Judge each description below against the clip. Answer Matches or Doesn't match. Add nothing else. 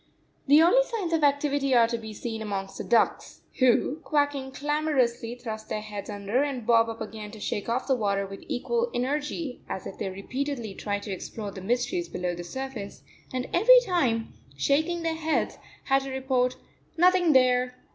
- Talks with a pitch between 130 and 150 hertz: Doesn't match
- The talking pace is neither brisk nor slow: Matches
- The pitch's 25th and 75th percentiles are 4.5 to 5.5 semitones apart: Matches